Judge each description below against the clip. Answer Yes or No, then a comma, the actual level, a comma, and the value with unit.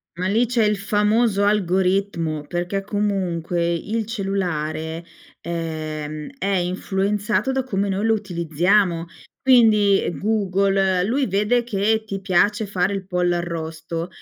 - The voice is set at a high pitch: Yes, high, 195 Hz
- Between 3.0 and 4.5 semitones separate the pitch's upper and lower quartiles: Yes, average, 3.3 semitones